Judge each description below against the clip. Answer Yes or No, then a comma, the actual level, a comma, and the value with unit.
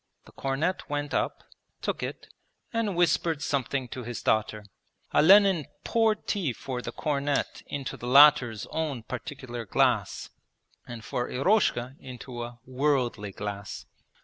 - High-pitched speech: No, low, 135 Hz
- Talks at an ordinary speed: No, slow, 130 wpm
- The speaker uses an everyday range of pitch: Yes, average, 4.1 semitones